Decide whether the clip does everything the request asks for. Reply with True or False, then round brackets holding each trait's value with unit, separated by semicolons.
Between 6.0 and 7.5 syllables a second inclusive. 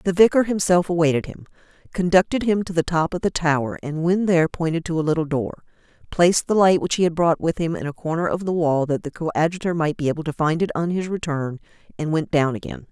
True (6.2 syllables/s)